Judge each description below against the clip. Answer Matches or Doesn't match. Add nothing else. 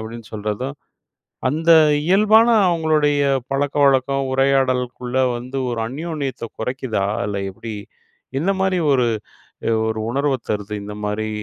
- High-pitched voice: Doesn't match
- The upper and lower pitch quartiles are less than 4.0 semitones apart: Doesn't match